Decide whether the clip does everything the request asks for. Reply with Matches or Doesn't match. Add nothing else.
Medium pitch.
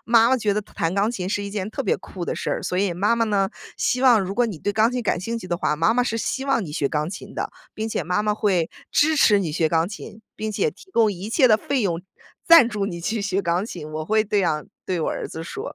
Doesn't match